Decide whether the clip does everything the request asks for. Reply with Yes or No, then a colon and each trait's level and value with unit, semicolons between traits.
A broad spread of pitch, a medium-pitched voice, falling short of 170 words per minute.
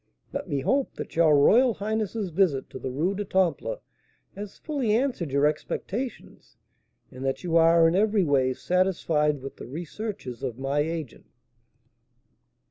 Yes: wide, 6.5 semitones; medium, 170 Hz; average, 150 wpm